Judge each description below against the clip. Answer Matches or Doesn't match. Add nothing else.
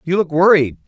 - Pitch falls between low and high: Matches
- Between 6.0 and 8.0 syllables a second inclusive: Doesn't match